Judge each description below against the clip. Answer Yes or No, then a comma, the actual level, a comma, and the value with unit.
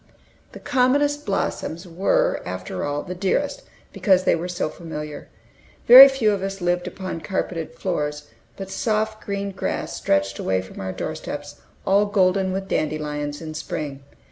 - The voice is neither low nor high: Yes, medium, 180 Hz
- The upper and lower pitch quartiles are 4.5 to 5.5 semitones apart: Yes, average, 4.8 semitones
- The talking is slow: No, average, 155 wpm